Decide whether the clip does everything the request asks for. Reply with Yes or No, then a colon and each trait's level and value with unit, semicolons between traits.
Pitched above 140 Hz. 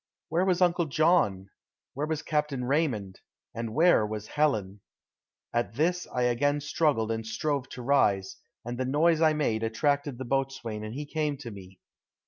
No: low, 135 Hz